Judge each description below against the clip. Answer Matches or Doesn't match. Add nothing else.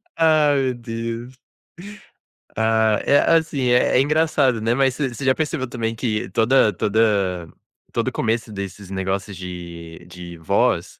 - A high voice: Doesn't match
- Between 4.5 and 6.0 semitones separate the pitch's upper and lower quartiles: Matches